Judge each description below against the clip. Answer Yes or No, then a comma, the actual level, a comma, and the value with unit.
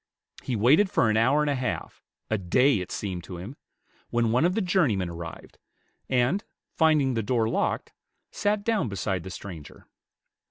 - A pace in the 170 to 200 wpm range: Yes, average, 175 wpm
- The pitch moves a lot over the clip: Yes, wide, 7.5 semitones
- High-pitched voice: No, low, 120 Hz